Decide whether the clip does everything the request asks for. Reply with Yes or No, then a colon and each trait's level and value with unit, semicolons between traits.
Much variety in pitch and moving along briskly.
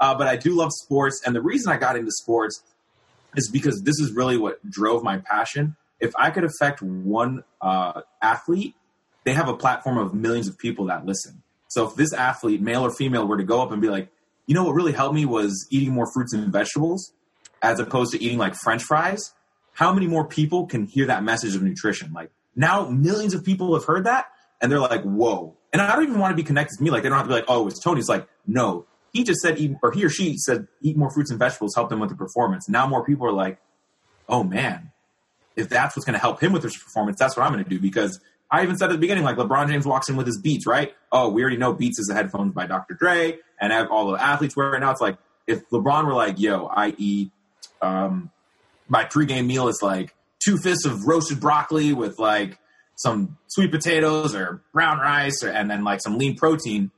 Yes: wide, 6.4 semitones; fast, 240 wpm